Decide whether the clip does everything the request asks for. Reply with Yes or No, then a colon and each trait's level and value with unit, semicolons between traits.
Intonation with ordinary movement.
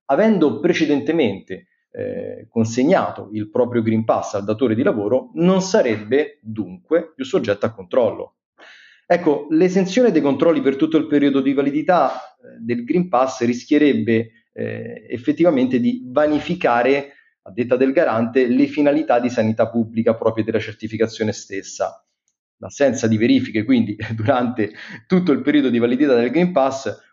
No: wide, 6.4 semitones